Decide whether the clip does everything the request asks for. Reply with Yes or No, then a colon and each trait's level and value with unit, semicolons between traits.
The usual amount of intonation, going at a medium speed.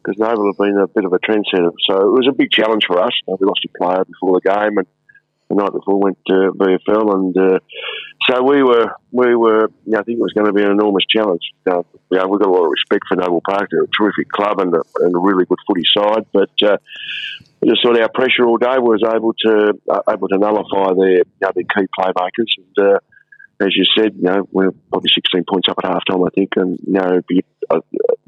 No: average, 3.3 semitones; fast, 255 wpm